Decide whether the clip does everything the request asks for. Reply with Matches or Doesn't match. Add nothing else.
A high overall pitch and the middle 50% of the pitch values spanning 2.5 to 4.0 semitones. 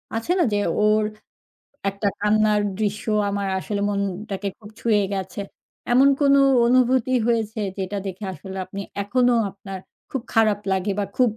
Matches